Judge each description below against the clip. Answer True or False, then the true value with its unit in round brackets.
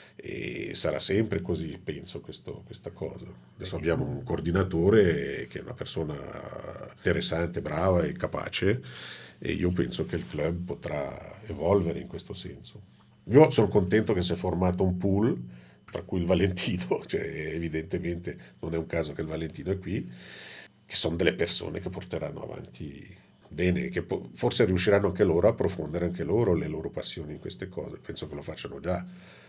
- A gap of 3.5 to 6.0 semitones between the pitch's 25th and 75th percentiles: False (2.6 semitones)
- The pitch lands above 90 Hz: False (85 Hz)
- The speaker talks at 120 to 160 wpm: False (170 wpm)